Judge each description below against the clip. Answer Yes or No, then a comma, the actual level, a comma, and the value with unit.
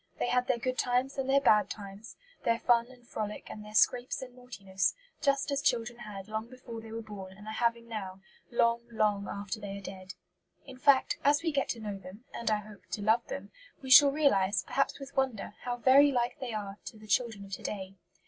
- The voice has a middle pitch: No, high, 230 Hz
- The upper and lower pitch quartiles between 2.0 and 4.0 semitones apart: Yes, average, 3.6 semitones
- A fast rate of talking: Yes, fast, 225 wpm